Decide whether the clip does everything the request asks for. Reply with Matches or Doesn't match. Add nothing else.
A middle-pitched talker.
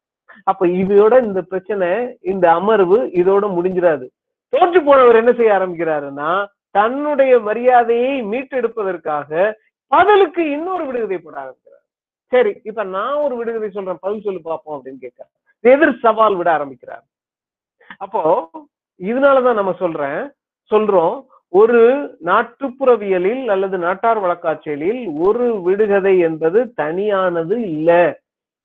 Doesn't match